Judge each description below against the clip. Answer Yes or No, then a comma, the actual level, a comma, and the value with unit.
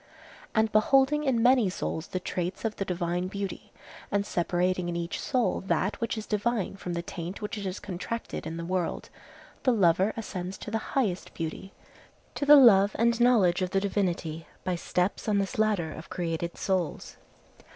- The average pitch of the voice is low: No, high, 195 Hz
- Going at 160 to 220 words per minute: Yes, average, 180 wpm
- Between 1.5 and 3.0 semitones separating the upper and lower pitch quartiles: No, average, 3.8 semitones